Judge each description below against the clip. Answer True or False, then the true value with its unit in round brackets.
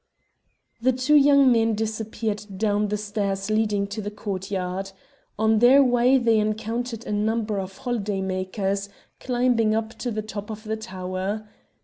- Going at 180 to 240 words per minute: False (145 wpm)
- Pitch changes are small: True (2.3 semitones)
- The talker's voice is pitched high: True (215 Hz)